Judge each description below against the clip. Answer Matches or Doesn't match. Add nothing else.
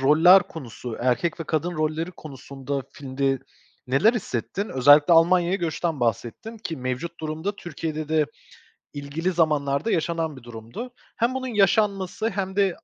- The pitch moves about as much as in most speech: Matches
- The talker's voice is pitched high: Doesn't match